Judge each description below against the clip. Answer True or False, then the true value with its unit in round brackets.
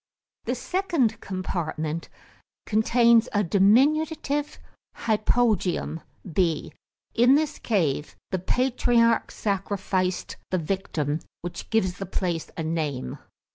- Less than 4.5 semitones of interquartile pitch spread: False (5.6 semitones)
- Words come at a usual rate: False (95 wpm)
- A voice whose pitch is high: True (200 Hz)